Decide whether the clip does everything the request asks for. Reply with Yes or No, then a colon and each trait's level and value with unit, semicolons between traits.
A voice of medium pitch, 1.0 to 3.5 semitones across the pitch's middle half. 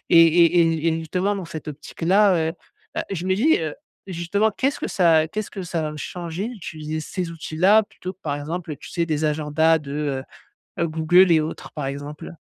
Yes: medium, 165 Hz; average, 3.0 semitones